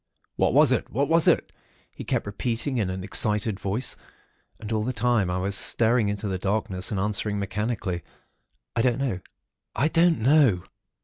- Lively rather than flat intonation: No, average, 3.8 semitones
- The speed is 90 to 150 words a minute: No, average, 175 wpm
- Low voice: Yes, low, 105 Hz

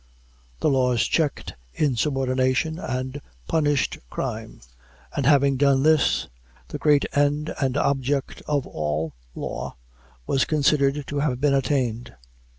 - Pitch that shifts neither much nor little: No, narrow, 2.2 semitones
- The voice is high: No, medium, 140 Hz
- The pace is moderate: No, slow, 120 wpm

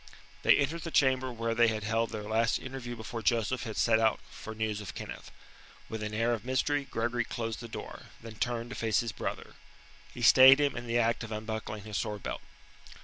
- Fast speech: Yes, fast, 210 wpm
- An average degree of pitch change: No, narrow, 1.8 semitones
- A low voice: Yes, low, 115 Hz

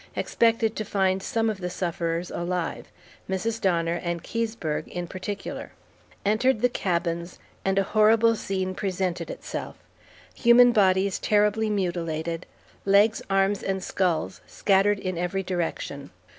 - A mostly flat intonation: No, average, 3.4 semitones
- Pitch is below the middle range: No, high, 190 Hz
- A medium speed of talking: No, slow, 130 wpm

